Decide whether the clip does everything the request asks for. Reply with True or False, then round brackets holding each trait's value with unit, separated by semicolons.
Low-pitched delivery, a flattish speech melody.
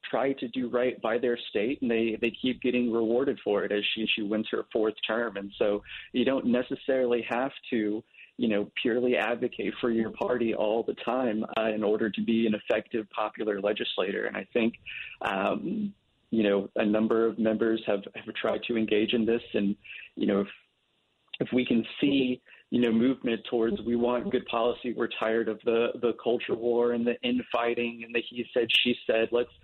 True (115 Hz; 1.8 semitones)